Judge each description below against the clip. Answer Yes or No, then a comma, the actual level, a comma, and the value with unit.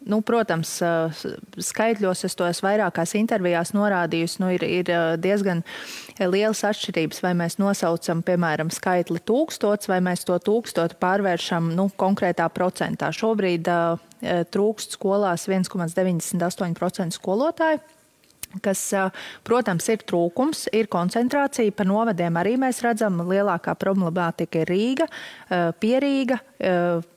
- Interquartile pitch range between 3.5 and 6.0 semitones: Yes, average, 3.9 semitones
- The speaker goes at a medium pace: No, slow, 115 wpm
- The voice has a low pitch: No, high, 190 Hz